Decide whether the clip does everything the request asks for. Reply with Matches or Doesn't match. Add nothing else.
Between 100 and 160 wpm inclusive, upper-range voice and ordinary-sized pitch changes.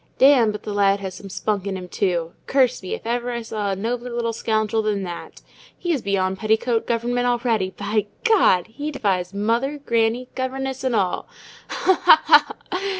Doesn't match